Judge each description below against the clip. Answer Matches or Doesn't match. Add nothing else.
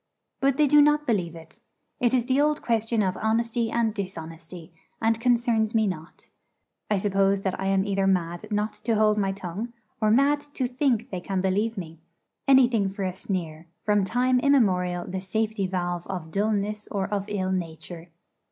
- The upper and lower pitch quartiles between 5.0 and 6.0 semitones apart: Doesn't match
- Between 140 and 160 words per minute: Doesn't match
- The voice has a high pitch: Matches